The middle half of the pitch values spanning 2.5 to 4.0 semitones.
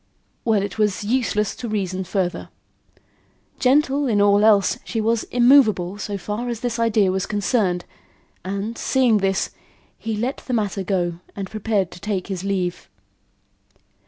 Yes: average, 3.1 semitones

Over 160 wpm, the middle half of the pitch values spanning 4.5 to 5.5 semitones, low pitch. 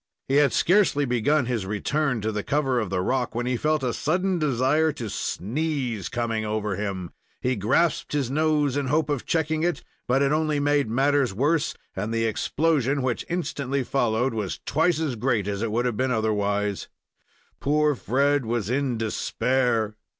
Yes: average, 180 wpm; average, 4.8 semitones; low, 130 Hz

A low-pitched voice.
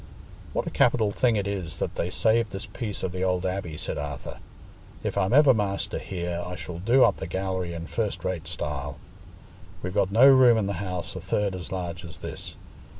Yes: very low, 95 Hz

